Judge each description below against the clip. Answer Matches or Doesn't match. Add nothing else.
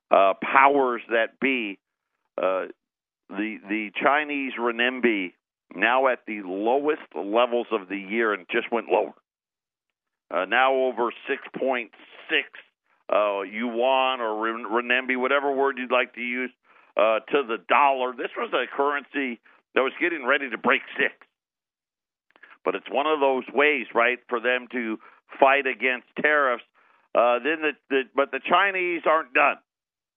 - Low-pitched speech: Matches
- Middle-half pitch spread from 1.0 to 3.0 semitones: Matches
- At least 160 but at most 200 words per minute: Doesn't match